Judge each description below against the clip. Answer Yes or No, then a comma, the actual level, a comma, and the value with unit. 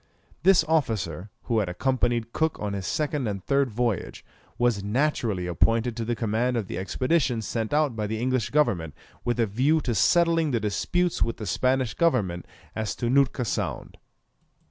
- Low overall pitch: Yes, low, 120 Hz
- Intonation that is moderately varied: Yes, average, 4.7 semitones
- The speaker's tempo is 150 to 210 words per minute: Yes, average, 170 wpm